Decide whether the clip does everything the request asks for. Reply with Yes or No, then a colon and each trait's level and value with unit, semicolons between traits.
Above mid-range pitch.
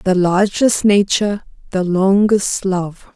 Yes: high, 195 Hz